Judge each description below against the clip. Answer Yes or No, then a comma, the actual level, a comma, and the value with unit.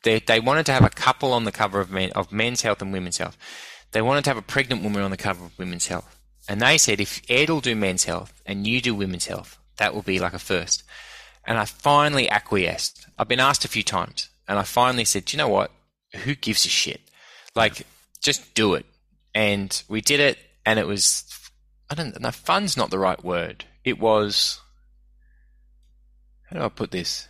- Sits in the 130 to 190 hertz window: No, low, 105 Hz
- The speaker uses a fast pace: Yes, fast, 215 wpm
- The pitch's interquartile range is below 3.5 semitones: No, average, 4.4 semitones